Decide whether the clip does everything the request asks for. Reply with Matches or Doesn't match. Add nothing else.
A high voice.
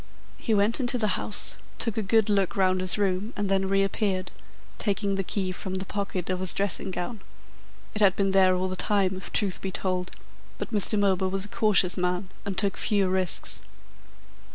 Matches